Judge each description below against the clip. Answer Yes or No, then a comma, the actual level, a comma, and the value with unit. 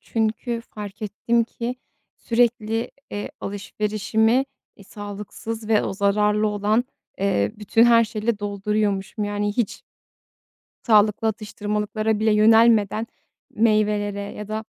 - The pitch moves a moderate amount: No, narrow, 1.5 semitones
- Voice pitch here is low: No, high, 215 Hz